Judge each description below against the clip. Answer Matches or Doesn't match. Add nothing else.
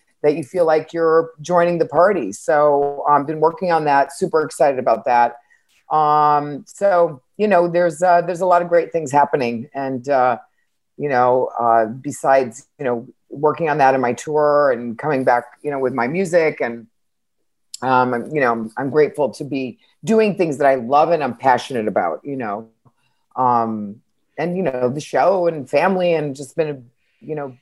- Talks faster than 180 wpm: Matches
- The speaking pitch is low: Doesn't match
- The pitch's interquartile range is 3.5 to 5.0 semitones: Matches